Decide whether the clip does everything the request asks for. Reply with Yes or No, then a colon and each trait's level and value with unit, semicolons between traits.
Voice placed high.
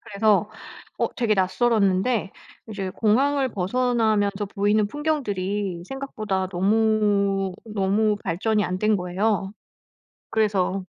Yes: high, 205 Hz